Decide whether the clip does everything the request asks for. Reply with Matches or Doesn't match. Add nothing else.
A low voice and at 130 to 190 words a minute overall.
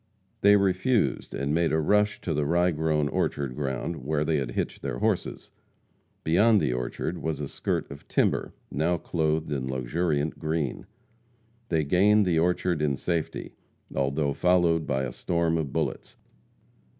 Matches